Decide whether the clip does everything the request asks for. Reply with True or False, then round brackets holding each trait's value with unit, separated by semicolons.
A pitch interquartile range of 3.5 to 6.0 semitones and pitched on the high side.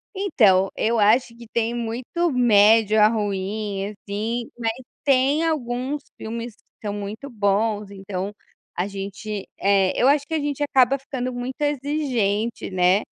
True (4.2 semitones; 225 Hz)